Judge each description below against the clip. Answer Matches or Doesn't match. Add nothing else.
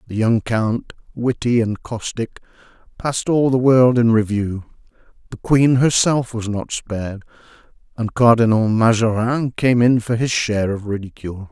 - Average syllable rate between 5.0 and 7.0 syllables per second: Doesn't match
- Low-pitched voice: Matches